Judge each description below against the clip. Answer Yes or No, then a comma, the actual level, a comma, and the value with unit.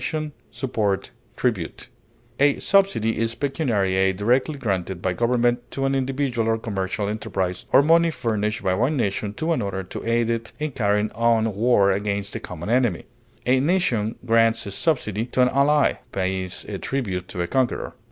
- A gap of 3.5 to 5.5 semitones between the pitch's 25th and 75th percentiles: Yes, average, 4.8 semitones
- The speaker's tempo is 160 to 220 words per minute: Yes, average, 170 wpm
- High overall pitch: No, low, 115 Hz